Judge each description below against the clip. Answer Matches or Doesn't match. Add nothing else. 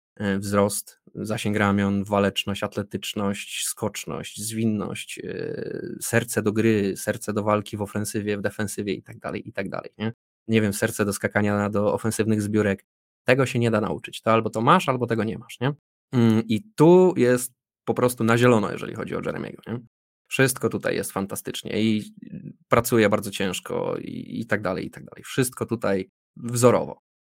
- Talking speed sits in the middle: Doesn't match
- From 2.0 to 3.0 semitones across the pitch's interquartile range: Matches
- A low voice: Matches